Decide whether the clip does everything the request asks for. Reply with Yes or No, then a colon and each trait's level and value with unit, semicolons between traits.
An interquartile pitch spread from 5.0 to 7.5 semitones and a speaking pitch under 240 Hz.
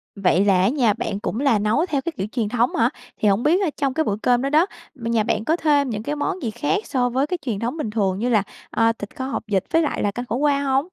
No: average, 5.3 semitones; high, 245 Hz